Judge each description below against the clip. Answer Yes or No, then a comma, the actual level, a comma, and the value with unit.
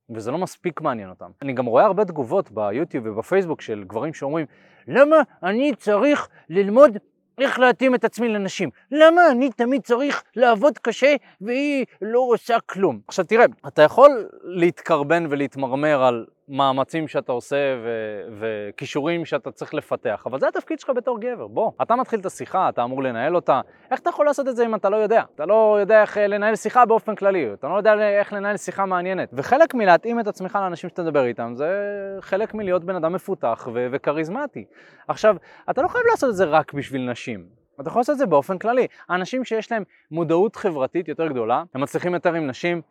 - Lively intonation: Yes, wide, 7.6 semitones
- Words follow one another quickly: Yes, fast, 185 wpm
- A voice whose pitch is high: Yes, high, 195 Hz